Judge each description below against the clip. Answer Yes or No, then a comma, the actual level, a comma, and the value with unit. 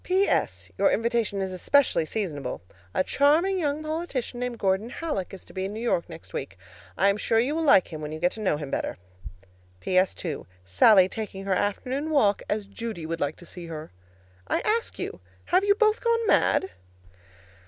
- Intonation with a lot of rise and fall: Yes, wide, 7.9 semitones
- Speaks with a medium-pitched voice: No, high, 210 Hz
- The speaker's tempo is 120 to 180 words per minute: No, average, 190 wpm